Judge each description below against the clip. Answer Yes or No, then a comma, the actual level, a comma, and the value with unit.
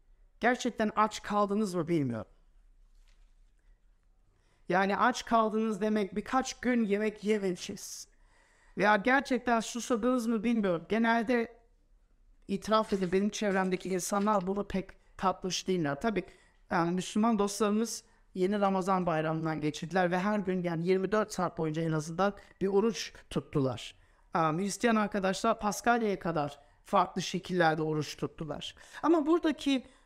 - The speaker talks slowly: No, average, 120 wpm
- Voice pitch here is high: Yes, high, 200 Hz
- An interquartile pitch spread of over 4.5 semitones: No, average, 4.0 semitones